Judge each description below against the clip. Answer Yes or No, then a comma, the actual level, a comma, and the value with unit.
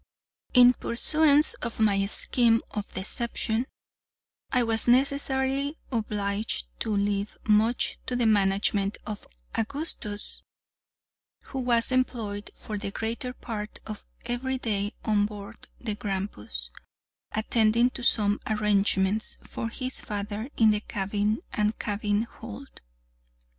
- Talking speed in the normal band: No, slow, 115 wpm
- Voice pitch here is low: No, high, 220 Hz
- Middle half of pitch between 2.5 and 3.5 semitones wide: Yes, average, 2.9 semitones